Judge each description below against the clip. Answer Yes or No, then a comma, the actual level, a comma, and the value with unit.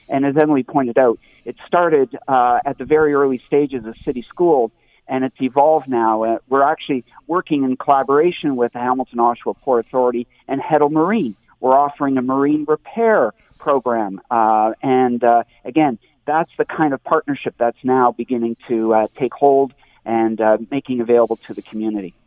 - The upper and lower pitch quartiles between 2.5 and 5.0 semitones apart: Yes, average, 3.5 semitones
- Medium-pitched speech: No, low, 130 Hz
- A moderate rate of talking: Yes, average, 170 wpm